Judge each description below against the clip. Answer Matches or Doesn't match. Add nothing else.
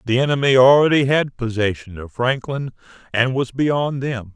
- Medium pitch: Doesn't match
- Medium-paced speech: Matches